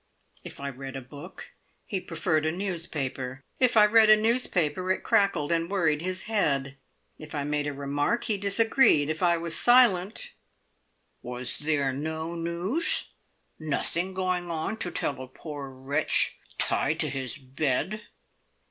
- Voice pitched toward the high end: No, medium, 165 Hz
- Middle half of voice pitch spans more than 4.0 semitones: Yes, average, 5.2 semitones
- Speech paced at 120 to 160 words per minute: Yes, average, 150 wpm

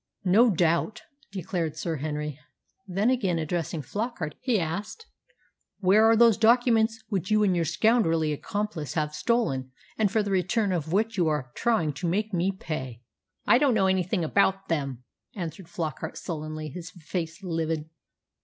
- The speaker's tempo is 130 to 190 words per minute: Yes, average, 155 wpm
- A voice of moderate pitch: Yes, medium, 180 Hz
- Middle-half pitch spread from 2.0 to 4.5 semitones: No, average, 5.2 semitones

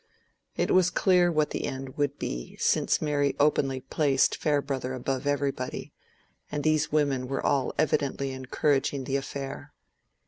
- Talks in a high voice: No, medium, 140 Hz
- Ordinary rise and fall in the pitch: No, narrow, 1.8 semitones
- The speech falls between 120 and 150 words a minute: Yes, average, 140 wpm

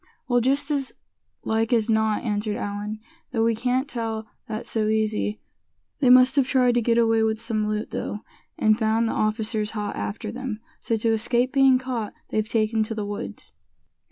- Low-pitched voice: No, high, 225 Hz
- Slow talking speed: No, average, 185 wpm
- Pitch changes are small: Yes, narrow, 2.2 semitones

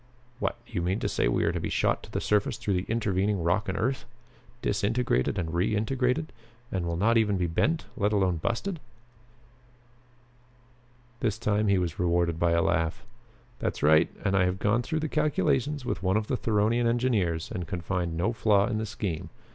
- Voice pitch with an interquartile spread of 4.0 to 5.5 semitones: Yes, average, 4.9 semitones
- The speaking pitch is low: Yes, low, 100 Hz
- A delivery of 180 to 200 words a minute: Yes, average, 190 wpm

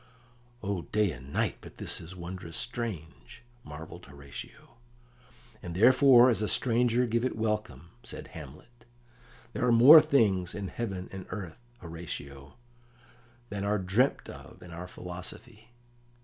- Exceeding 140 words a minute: No, slow, 135 wpm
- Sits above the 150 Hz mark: No, low, 100 Hz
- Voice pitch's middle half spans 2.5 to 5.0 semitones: No, wide, 5.6 semitones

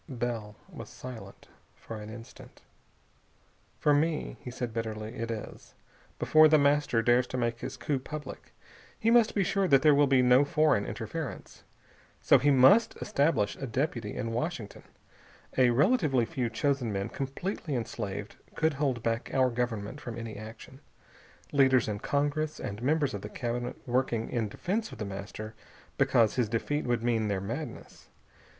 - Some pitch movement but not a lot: Yes, average, 4.4 semitones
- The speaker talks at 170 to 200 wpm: No, average, 160 wpm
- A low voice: Yes, low, 125 Hz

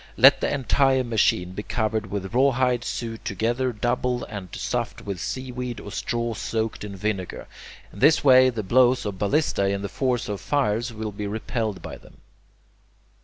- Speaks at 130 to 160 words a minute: No, average, 170 wpm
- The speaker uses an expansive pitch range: No, average, 3.7 semitones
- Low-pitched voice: Yes, low, 115 Hz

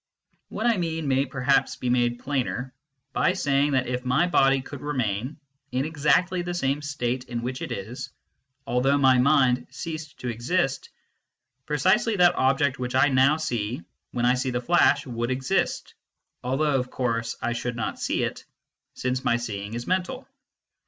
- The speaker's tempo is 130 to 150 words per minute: No, average, 170 wpm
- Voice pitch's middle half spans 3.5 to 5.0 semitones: No, average, 3.1 semitones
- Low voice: Yes, low, 130 Hz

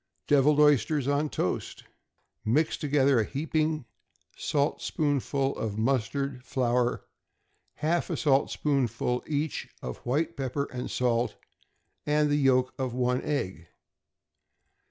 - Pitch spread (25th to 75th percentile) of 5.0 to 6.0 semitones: No, average, 3.0 semitones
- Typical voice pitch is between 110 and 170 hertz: Yes, low, 135 Hz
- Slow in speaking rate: Yes, slow, 110 wpm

